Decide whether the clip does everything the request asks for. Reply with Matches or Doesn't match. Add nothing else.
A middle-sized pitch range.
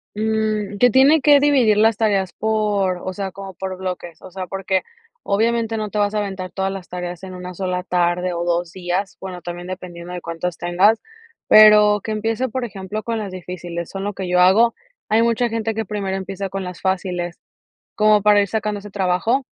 Matches